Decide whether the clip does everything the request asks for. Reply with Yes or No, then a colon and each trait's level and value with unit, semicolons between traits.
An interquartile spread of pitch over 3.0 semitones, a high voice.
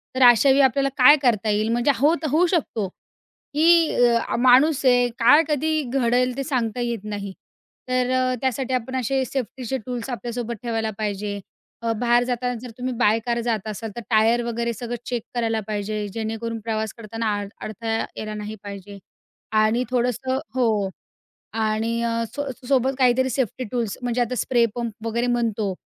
No: narrow, 2.6 semitones; high, 235 Hz